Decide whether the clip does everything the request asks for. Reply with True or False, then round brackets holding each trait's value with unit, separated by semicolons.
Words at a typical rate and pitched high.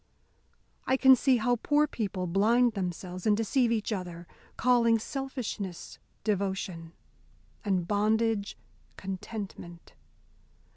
False (100 wpm; 210 Hz)